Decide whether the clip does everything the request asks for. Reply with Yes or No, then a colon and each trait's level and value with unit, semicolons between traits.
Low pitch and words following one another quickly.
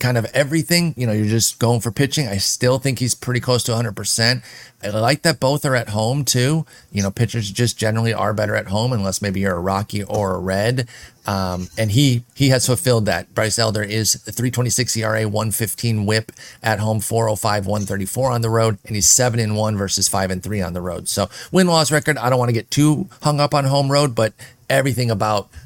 Yes: low, 115 Hz; fast, 220 wpm